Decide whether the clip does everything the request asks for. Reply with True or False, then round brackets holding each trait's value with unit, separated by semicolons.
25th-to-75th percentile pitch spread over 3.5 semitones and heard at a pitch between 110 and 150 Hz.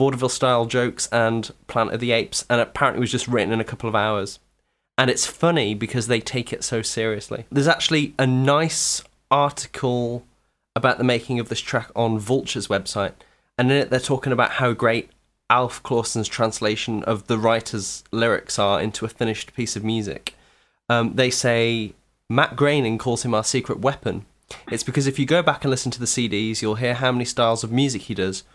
False (2.5 semitones; 120 Hz)